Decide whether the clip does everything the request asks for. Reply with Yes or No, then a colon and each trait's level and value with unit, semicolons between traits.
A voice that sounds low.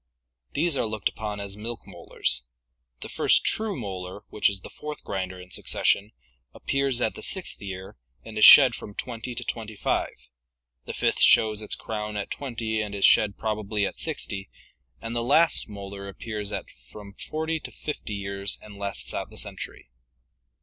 Yes: low, 105 Hz